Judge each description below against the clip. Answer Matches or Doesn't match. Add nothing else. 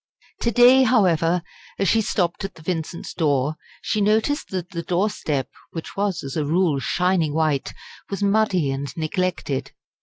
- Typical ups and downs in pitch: Matches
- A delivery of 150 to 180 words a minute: Matches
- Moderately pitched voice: Matches